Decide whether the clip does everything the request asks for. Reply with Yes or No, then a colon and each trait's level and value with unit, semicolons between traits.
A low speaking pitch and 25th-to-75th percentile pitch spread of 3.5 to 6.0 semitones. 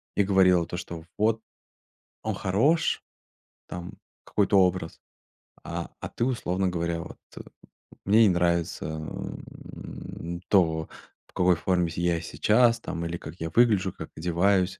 No: very low, 90 Hz; average, 2.8 semitones